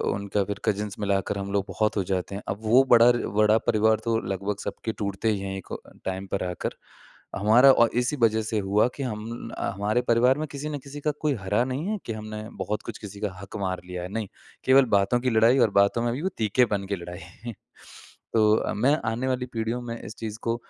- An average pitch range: Yes, average, 3.4 semitones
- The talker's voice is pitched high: No, low, 110 Hz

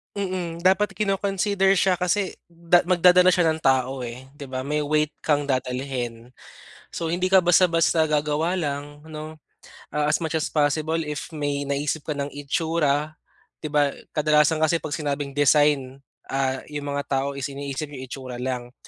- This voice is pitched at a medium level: Yes, medium, 150 Hz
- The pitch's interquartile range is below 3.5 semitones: Yes, average, 3.1 semitones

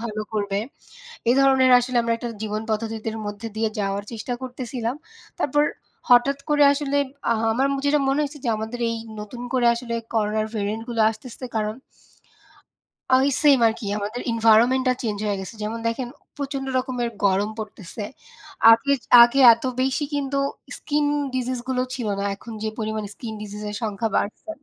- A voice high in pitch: Yes, high, 230 Hz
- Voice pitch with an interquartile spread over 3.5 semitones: No, average, 3.2 semitones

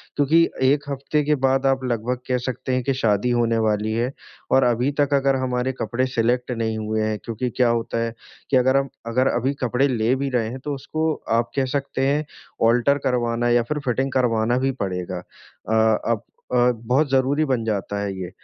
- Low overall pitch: Yes, low, 125 Hz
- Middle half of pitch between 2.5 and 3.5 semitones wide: Yes, average, 2.9 semitones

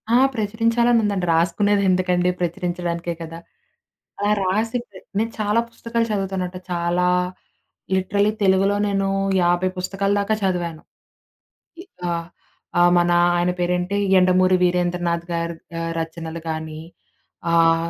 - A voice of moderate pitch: Yes, medium, 180 Hz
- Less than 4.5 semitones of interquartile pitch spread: Yes, average, 2.8 semitones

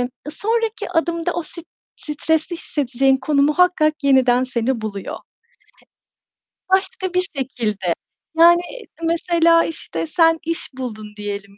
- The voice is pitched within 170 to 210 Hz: No, very high, 300 Hz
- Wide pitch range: Yes, wide, 5.7 semitones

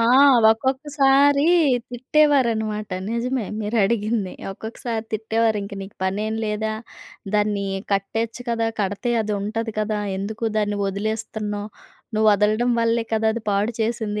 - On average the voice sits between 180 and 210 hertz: No, high, 220 Hz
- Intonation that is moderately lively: No, narrow, 2.0 semitones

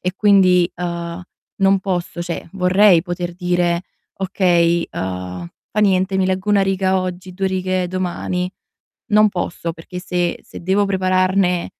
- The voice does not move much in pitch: Yes, narrow, 1.5 semitones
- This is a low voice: No, medium, 185 Hz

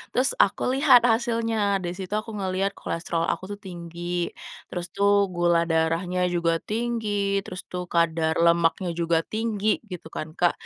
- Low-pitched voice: No, medium, 180 Hz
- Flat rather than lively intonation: No, average, 3.6 semitones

